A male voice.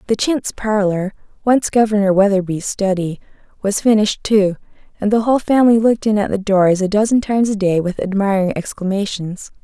No: female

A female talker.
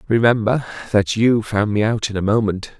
No: male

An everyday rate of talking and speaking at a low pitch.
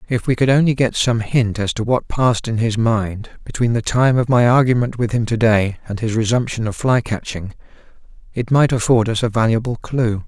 No: fast, 215 wpm; low, 115 Hz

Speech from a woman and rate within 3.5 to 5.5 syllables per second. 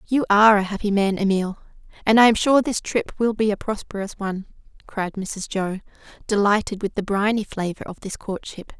Yes: female; 5.2 syllables/s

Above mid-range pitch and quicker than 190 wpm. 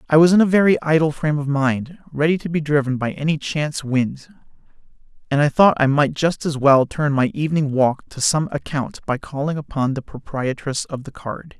No: medium, 145 Hz; fast, 205 wpm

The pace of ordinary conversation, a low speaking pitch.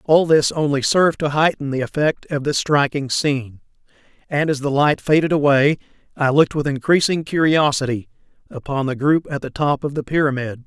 No: average, 180 wpm; medium, 145 Hz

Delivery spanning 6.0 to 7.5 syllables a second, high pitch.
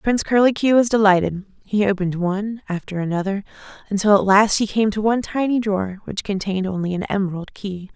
Yes: 6.2 syllables/s; high, 200 Hz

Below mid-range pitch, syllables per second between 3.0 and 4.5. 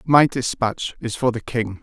Yes: low, 120 Hz; 4.1 syllables/s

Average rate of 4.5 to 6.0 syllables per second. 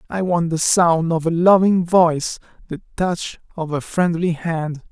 No: 4.2 syllables/s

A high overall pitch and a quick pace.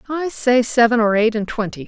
Yes: high, 235 Hz; fast, 225 wpm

